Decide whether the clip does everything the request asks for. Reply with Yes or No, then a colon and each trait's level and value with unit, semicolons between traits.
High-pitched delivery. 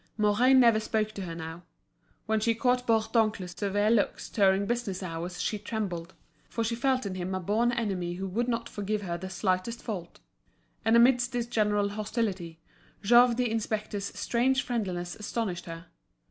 Yes: high, 210 Hz